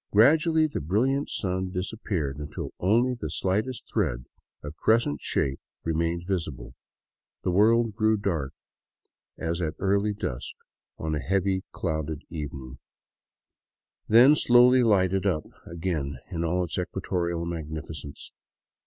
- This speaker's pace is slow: Yes, slow, 120 wpm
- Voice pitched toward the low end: Yes, very low, 90 Hz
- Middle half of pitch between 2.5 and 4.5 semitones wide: No, wide, 5.5 semitones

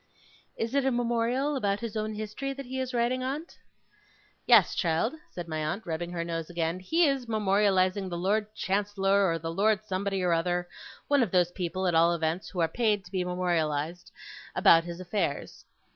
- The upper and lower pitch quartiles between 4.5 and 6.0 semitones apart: Yes, average, 4.8 semitones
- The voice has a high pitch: Yes, high, 195 Hz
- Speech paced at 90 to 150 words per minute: No, average, 190 wpm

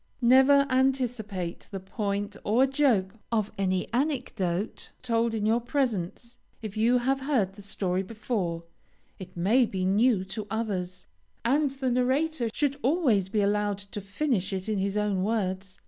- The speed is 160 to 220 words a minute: No, average, 150 wpm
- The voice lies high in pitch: Yes, high, 215 Hz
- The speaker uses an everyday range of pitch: Yes, average, 4.7 semitones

